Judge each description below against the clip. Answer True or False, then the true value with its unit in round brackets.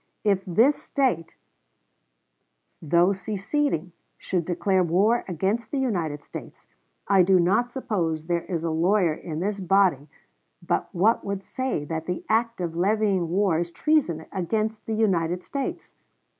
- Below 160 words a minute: True (145 wpm)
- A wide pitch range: False (4.2 semitones)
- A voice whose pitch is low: False (190 Hz)